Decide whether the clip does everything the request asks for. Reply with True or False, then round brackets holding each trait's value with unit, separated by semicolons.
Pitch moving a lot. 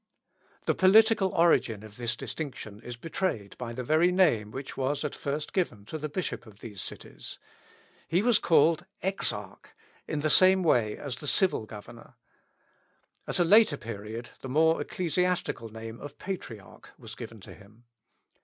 True (7.9 semitones)